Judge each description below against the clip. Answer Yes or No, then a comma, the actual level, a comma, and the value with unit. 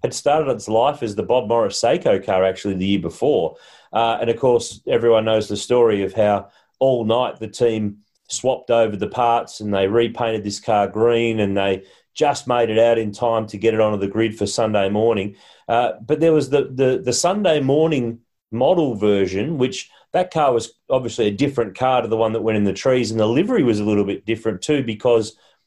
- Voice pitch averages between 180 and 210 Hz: No, low, 115 Hz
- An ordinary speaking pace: No, fast, 215 wpm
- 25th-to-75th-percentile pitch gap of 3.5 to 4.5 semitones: No, average, 2.9 semitones